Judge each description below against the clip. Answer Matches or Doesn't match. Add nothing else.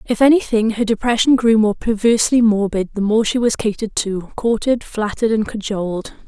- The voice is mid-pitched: Doesn't match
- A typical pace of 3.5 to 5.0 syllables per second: Doesn't match